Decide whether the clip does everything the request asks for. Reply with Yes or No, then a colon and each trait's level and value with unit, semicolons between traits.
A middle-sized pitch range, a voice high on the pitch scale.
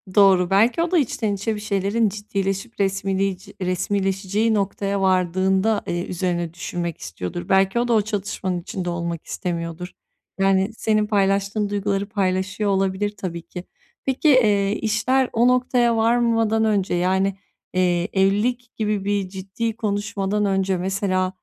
No: narrow, 2.3 semitones; high, 195 Hz